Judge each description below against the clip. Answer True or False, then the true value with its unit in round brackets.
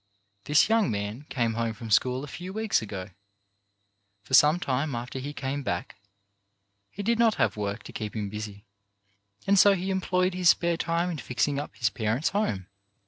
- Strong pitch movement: True (8.5 semitones)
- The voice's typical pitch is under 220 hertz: True (140 Hz)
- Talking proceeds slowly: False (185 wpm)